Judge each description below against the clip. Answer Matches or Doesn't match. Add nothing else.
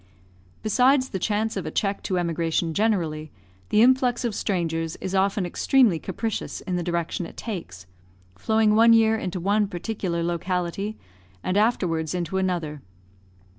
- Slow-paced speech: Doesn't match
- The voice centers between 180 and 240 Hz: Matches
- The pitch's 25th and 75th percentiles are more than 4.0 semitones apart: Matches